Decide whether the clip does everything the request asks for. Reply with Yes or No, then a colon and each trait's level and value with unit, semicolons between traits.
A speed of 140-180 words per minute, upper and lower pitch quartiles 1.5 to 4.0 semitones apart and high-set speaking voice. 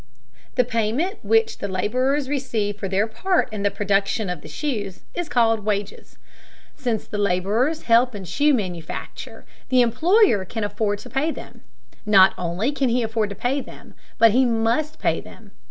No: average, 170 wpm; average, 4.6 semitones; high, 225 Hz